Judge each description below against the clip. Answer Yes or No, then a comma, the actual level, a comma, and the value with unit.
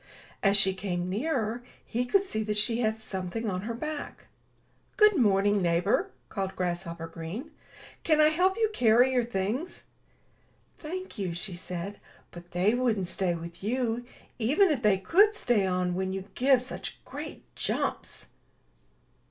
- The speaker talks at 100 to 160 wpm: Yes, average, 150 wpm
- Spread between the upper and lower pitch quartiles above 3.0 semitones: Yes, wide, 5.5 semitones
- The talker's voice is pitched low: No, high, 215 Hz